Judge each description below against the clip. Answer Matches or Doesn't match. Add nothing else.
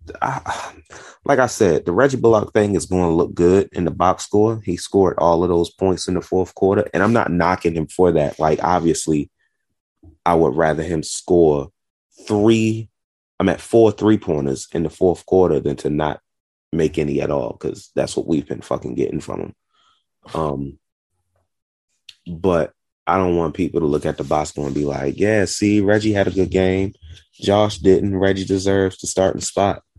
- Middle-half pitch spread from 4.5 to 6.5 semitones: Doesn't match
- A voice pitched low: Matches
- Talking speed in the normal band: Matches